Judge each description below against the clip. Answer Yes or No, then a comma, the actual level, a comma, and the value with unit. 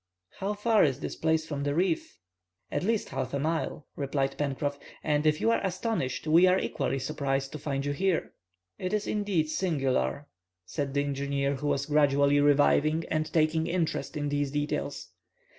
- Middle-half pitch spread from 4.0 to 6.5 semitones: No, average, 3.1 semitones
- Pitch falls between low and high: Yes, medium, 150 Hz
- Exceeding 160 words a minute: Yes, average, 175 wpm